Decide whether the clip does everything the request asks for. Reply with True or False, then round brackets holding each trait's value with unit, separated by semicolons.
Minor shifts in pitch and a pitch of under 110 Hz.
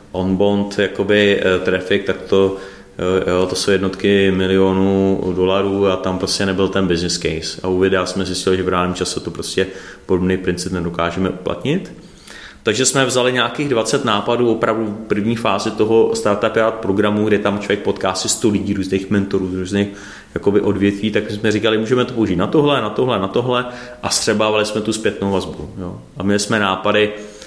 True (2.3 semitones; 100 Hz)